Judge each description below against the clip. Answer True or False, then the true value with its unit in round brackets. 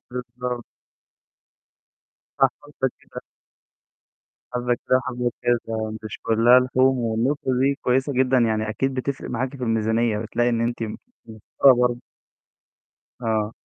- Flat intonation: True (2.3 semitones)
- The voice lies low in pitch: True (120 Hz)